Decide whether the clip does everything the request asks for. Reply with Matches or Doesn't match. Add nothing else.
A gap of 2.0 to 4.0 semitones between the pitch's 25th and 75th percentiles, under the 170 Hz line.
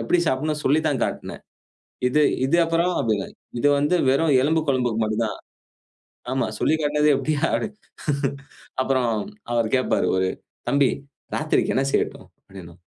Doesn't match